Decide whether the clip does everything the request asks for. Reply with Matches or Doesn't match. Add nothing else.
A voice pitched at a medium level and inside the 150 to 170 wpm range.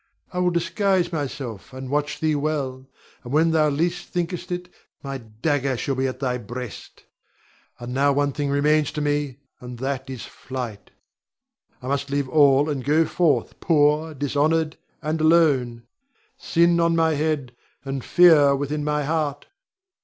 Matches